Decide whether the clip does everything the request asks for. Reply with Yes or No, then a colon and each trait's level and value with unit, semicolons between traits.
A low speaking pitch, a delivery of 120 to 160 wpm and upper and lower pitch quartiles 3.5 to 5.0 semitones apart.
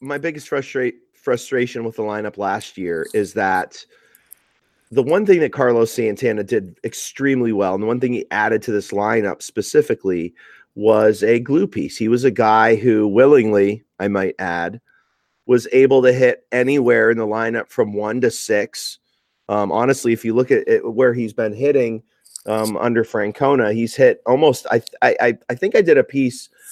No: low, 115 Hz; average, 180 wpm; average, 3.9 semitones